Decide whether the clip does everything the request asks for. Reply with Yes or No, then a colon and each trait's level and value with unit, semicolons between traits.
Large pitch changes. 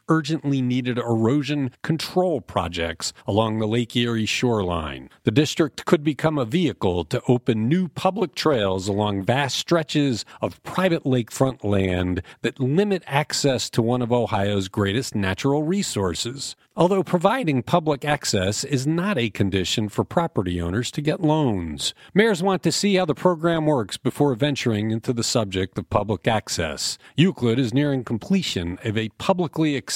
Yes: wide, 6.7 semitones